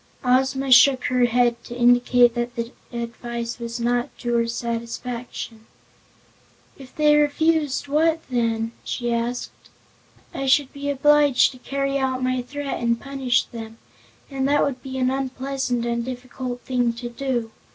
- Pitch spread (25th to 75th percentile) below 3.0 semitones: Yes, narrow, 2.4 semitones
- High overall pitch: Yes, very high, 250 Hz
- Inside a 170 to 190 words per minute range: No, average, 150 wpm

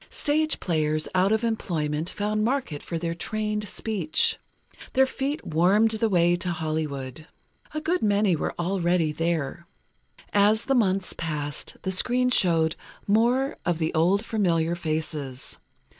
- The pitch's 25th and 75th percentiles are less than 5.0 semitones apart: No, average, 5.3 semitones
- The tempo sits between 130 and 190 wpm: Yes, average, 140 wpm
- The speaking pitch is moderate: Yes, medium, 180 Hz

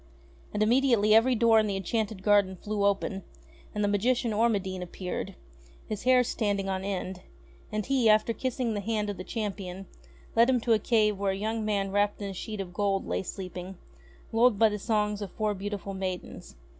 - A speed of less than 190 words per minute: No, average, 195 wpm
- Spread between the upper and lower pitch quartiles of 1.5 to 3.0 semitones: Yes, narrow, 2.4 semitones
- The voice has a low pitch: No, high, 205 Hz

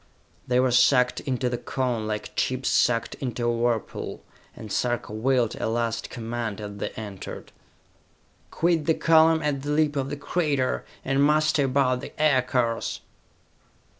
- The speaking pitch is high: No, low, 125 Hz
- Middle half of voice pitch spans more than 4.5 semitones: No, average, 3.6 semitones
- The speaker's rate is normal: Yes, average, 150 wpm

